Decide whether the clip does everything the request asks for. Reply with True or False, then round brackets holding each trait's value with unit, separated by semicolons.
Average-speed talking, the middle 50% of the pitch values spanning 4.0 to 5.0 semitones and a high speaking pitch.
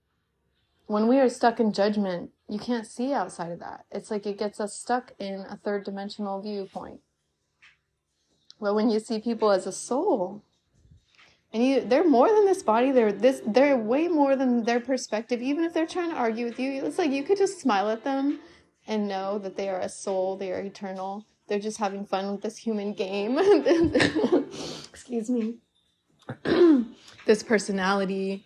True (180 wpm; 4.3 semitones; 215 Hz)